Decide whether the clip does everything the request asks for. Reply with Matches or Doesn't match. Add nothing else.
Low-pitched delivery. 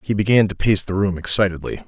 Matches